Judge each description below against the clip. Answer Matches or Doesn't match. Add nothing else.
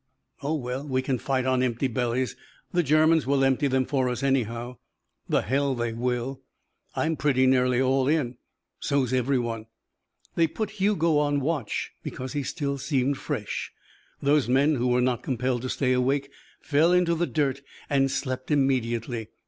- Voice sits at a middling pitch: Doesn't match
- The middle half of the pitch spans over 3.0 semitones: Doesn't match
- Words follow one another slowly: Doesn't match